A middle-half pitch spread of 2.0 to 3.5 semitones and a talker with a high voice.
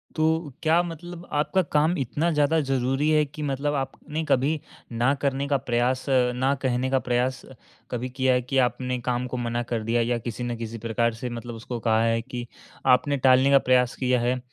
No: average, 2.9 semitones; low, 130 Hz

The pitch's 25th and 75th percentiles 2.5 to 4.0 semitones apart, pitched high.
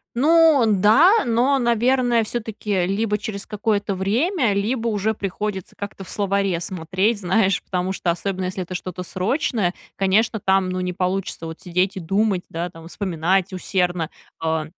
Yes: average, 3.4 semitones; high, 195 Hz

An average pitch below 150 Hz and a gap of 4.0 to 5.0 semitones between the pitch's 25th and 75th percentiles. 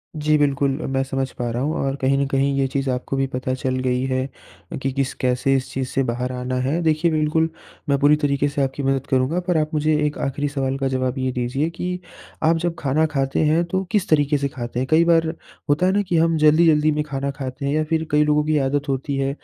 No: medium, 140 Hz; narrow, 2.6 semitones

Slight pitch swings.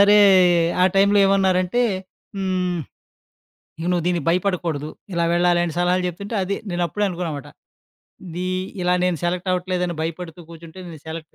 Yes: narrow, 1.4 semitones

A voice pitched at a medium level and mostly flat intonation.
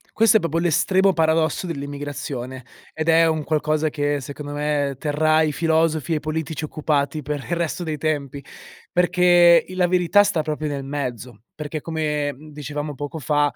Yes: medium, 155 Hz; narrow, 2.1 semitones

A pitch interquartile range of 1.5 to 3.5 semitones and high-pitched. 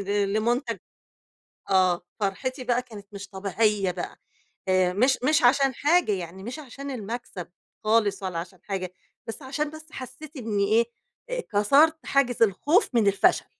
No: average, 5.3 semitones; high, 225 Hz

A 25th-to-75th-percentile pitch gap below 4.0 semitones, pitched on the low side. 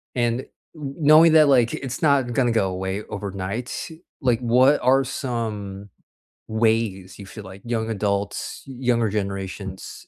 No: average, 4.4 semitones; low, 115 Hz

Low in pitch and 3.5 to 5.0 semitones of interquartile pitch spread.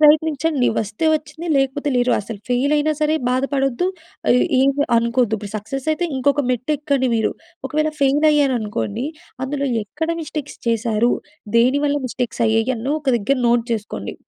No: very high, 265 Hz; average, 4.0 semitones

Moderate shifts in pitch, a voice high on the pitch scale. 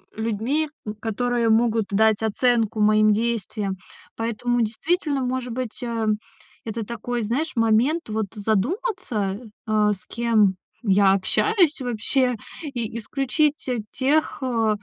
Yes: average, 3.1 semitones; high, 230 Hz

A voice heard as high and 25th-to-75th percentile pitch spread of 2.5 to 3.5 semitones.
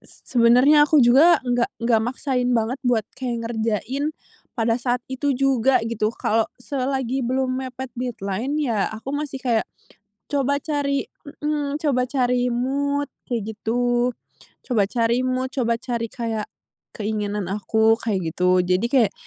Yes: high, 245 Hz; average, 2.9 semitones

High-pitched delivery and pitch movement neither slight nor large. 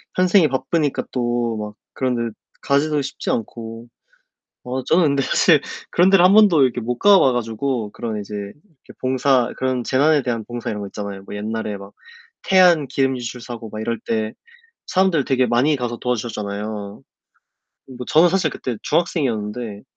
No: low, 125 Hz; average, 4.5 semitones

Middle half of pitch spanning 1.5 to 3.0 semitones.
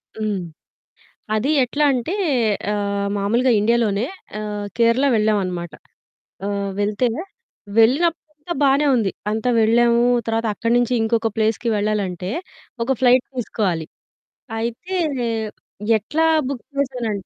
No: average, 3.4 semitones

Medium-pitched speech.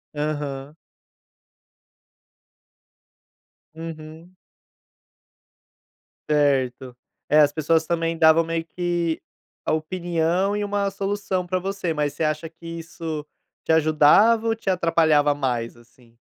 Yes: medium, 160 Hz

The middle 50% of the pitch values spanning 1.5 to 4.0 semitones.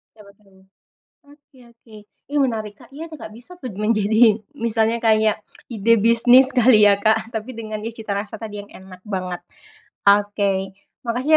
Yes: narrow, 2.4 semitones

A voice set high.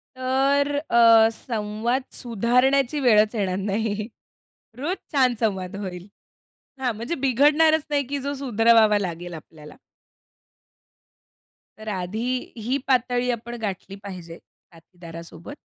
Yes: high, 230 Hz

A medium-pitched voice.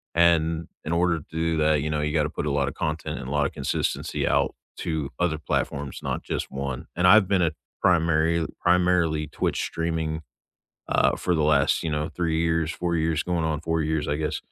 No: very low, 80 Hz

